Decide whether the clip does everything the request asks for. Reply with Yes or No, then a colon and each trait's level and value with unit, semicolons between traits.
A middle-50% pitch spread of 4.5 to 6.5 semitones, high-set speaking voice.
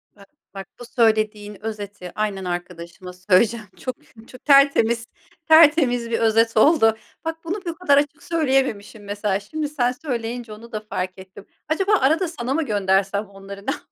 Yes: wide, 5.6 semitones; high, 225 Hz